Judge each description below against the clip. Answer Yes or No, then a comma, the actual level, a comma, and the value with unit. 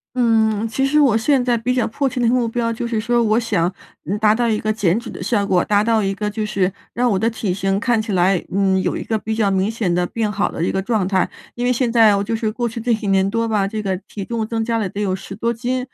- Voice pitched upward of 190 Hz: Yes, high, 220 Hz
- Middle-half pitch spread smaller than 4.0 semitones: Yes, average, 2.8 semitones